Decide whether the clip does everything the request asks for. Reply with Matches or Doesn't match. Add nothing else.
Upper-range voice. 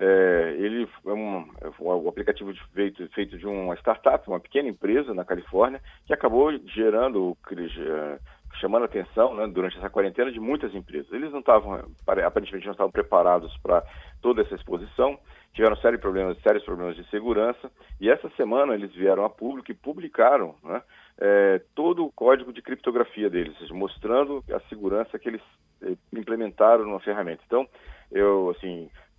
Doesn't match